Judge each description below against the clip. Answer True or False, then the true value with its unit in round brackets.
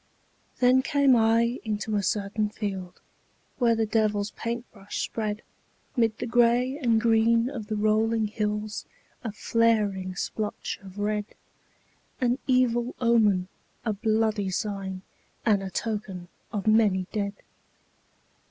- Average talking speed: False (125 wpm)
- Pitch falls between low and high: False (215 Hz)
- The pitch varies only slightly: True (2.1 semitones)